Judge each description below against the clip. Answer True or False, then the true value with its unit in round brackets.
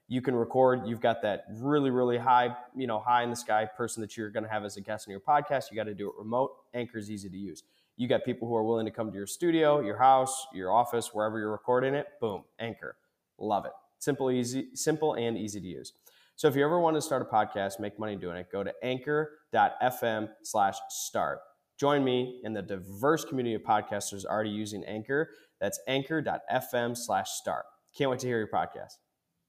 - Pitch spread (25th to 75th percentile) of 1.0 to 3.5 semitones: False (3.9 semitones)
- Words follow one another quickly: True (220 wpm)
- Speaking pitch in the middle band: False (120 Hz)